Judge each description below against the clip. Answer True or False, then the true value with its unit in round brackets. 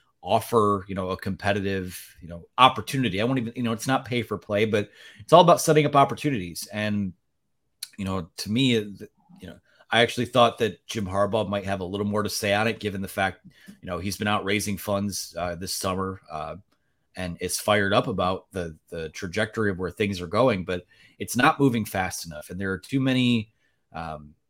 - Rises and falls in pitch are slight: False (3.5 semitones)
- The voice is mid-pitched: False (100 Hz)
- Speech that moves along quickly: True (210 wpm)